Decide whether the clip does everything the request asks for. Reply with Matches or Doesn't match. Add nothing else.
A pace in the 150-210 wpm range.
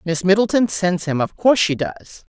Matches